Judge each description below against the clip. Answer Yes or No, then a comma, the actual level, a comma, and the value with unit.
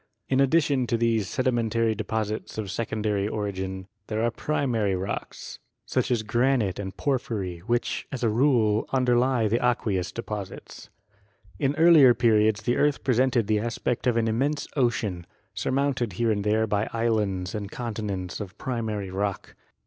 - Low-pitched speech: Yes, low, 110 Hz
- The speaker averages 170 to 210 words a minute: No, average, 150 wpm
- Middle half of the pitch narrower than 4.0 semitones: Yes, average, 3.2 semitones